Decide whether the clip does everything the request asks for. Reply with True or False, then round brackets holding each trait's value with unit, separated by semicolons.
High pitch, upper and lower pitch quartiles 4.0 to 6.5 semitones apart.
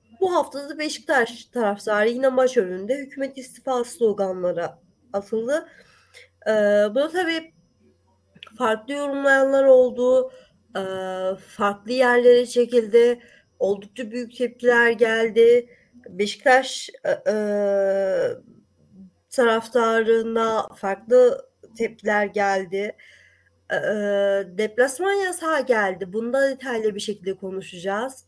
True (235 Hz; 4.4 semitones)